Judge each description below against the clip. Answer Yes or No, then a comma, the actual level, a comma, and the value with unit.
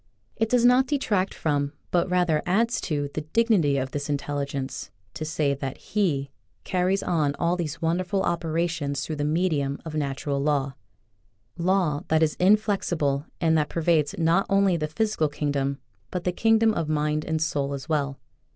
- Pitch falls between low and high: Yes, medium, 160 Hz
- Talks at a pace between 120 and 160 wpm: No, average, 170 wpm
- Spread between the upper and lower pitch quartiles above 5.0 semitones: No, average, 4.1 semitones